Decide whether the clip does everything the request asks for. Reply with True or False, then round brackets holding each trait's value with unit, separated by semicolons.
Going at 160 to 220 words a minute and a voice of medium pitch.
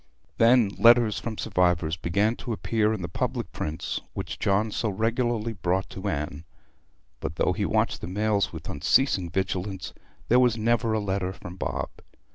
False (165 wpm; 100 Hz)